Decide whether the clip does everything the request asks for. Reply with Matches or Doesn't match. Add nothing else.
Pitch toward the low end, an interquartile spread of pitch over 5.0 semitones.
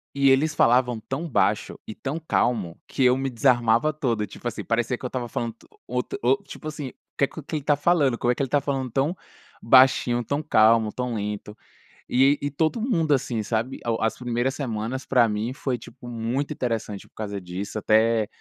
Doesn't match